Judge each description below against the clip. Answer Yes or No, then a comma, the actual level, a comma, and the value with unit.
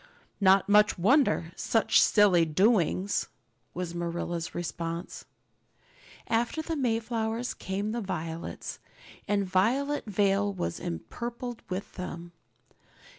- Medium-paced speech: No, slow, 100 wpm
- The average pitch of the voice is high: Yes, high, 200 Hz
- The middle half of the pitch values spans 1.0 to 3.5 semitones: No, average, 4.7 semitones